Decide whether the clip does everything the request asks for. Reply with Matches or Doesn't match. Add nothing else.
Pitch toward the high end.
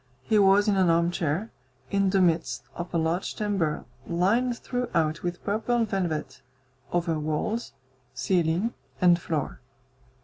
Doesn't match